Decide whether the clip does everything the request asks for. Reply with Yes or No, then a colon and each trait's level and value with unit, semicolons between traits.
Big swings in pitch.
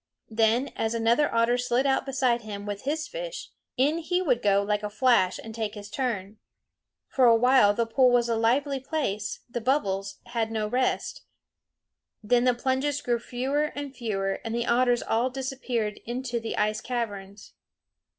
No: average, 3.3 semitones